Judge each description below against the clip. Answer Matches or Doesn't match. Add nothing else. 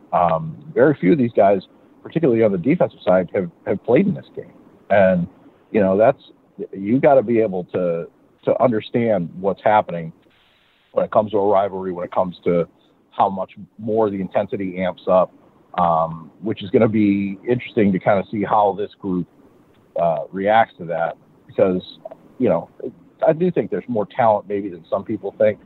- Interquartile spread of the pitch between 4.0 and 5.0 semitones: Doesn't match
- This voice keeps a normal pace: Matches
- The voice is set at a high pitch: Doesn't match